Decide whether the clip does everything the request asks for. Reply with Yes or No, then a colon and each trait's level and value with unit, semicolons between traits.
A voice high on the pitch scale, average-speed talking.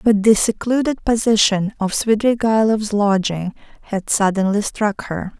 No: high, 210 Hz; slow, 120 wpm